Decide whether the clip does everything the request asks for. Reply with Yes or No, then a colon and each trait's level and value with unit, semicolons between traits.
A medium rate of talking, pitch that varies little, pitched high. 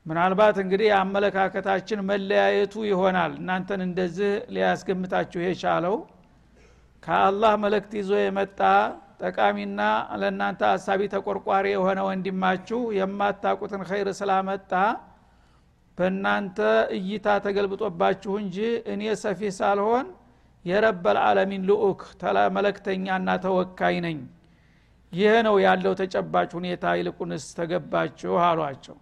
Yes: average, 90 wpm; narrow, 1.7 semitones; high, 195 Hz